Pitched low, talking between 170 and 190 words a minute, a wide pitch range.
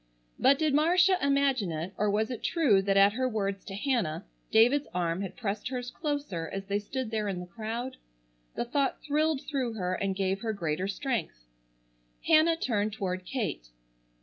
No: high, 220 Hz; average, 175 wpm; wide, 5.9 semitones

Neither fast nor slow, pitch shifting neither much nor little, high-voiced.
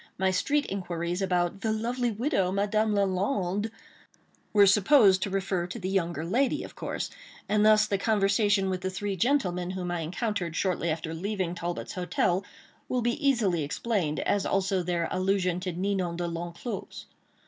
Yes: average, 160 wpm; average, 3.1 semitones; high, 195 Hz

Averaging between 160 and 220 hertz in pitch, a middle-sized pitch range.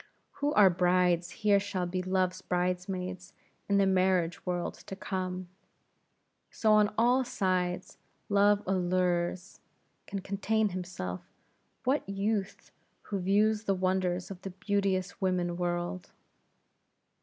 No: medium, 185 Hz; narrow, 1.8 semitones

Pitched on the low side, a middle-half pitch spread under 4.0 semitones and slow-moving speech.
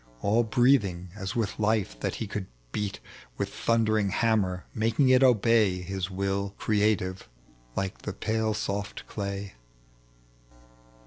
Yes: low, 105 Hz; narrow, 2.4 semitones; slow, 125 wpm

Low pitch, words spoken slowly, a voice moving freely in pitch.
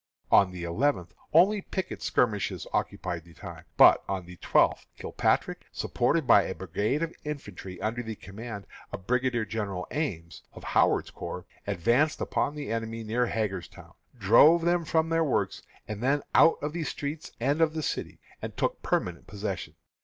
No: low, 115 Hz; average, 160 wpm; wide, 7.4 semitones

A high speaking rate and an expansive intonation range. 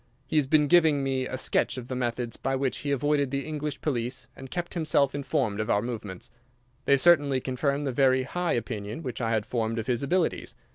No: fast, 210 wpm; average, 3.2 semitones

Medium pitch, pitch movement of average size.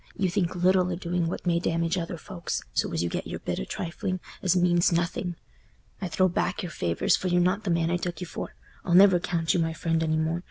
No: medium, 175 Hz; narrow, 1.5 semitones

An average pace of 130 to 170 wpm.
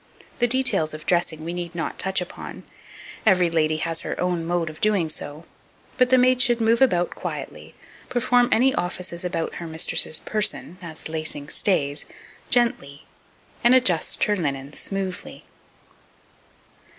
Yes: average, 145 wpm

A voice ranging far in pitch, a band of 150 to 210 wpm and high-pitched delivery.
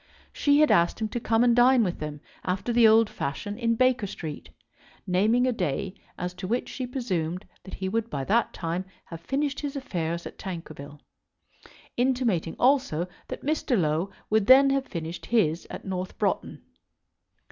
Yes: wide, 6.4 semitones; average, 170 wpm; high, 205 Hz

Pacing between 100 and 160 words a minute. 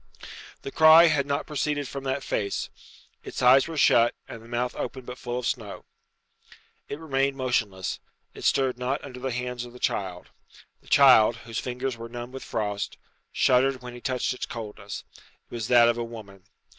No: average, 185 wpm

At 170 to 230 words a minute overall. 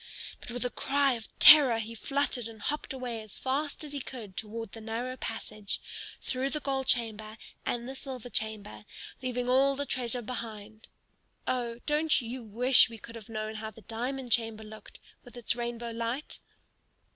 Yes: average, 175 wpm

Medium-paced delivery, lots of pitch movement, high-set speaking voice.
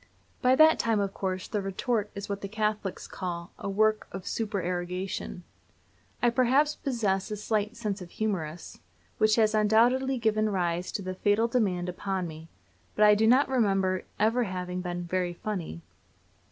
No: average, 165 wpm; average, 3.2 semitones; high, 205 Hz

